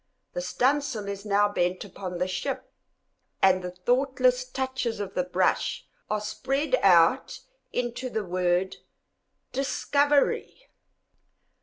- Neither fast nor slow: No, slow, 120 wpm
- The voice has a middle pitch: No, high, 215 Hz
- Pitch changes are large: Yes, wide, 5.9 semitones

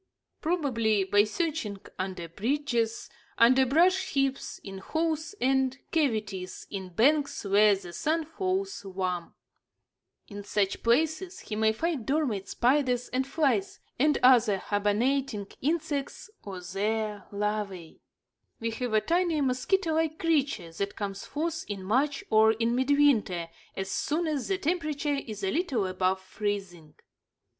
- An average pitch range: No, wide, 6.8 semitones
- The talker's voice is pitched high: Yes, high, 240 Hz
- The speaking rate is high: No, slow, 135 wpm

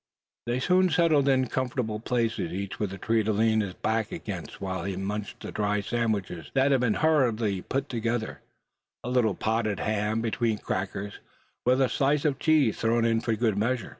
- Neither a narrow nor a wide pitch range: Yes, average, 3.6 semitones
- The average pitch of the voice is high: No, low, 115 Hz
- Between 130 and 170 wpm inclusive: No, average, 185 wpm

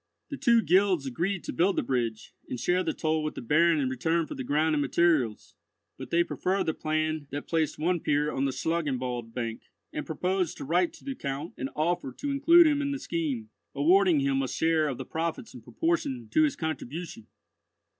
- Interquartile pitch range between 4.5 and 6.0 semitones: Yes, average, 4.9 semitones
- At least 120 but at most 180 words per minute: No, fast, 205 wpm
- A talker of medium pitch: Yes, medium, 160 Hz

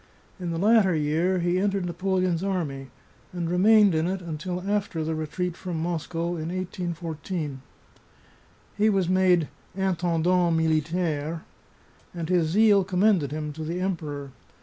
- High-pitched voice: No, medium, 175 Hz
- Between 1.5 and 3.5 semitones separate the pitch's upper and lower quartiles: Yes, average, 2.7 semitones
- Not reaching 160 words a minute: Yes, average, 140 wpm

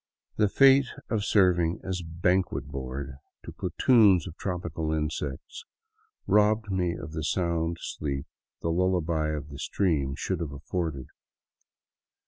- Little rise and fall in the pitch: No, average, 3.6 semitones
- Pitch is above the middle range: No, very low, 85 Hz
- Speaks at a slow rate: Yes, slow, 125 wpm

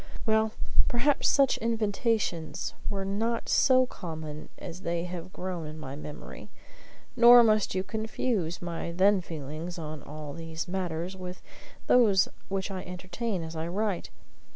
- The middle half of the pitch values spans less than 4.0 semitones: No, average, 4.9 semitones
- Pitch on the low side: No, medium, 185 Hz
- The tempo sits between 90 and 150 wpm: Yes, average, 140 wpm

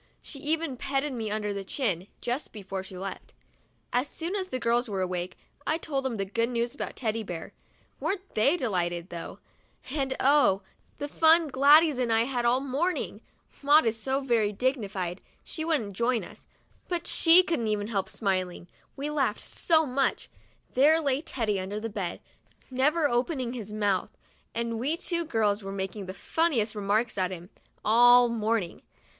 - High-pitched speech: Yes, high, 235 Hz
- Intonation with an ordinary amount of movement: No, wide, 5.7 semitones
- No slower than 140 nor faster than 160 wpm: No, average, 170 wpm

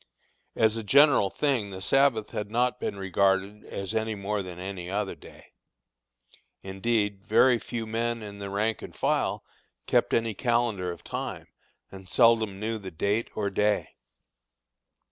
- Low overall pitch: Yes, low, 105 Hz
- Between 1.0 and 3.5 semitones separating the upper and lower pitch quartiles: Yes, average, 2.7 semitones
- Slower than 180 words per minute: Yes, average, 150 wpm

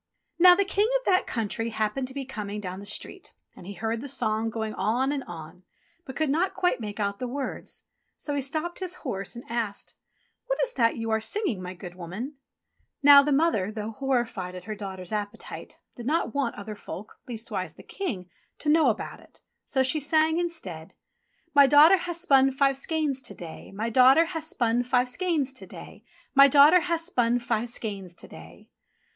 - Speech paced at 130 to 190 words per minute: No, average, 200 wpm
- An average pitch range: No, wide, 6.0 semitones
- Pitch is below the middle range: No, very high, 250 Hz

